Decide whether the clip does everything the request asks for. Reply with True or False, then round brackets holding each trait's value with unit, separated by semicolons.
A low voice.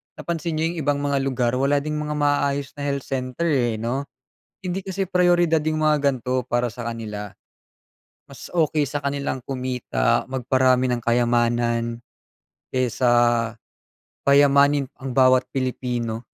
True (130 Hz)